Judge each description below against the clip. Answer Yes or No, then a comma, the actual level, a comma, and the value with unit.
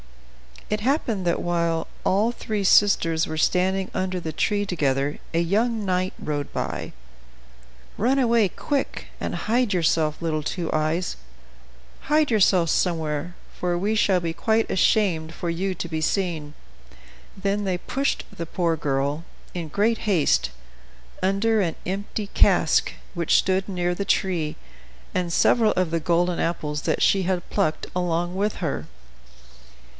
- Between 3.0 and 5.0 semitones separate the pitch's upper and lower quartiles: Yes, average, 3.7 semitones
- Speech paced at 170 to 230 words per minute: No, average, 145 wpm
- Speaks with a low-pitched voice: No, medium, 180 Hz